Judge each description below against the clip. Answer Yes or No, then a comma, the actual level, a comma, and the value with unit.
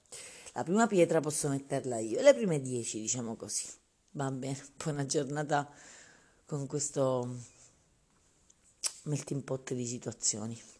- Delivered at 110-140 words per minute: Yes, average, 120 wpm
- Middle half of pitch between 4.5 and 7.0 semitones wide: No, average, 3.5 semitones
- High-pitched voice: No, medium, 140 Hz